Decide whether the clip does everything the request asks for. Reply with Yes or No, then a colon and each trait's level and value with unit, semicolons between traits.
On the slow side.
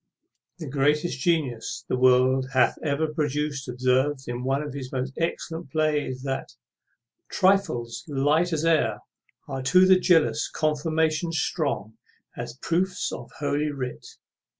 Yes: slow, 130 wpm